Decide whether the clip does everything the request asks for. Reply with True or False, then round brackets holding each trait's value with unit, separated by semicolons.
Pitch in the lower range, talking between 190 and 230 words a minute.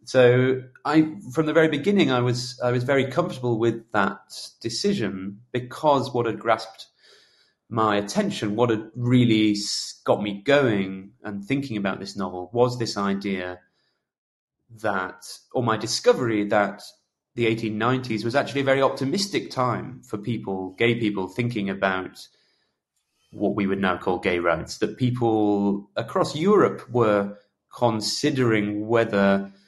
False (110 Hz; 135 wpm)